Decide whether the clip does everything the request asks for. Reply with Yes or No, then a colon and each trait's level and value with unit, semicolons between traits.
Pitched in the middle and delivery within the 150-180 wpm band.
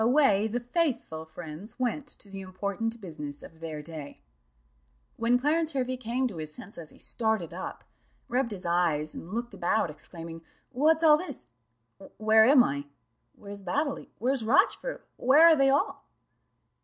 No: high, 220 Hz; average, 155 wpm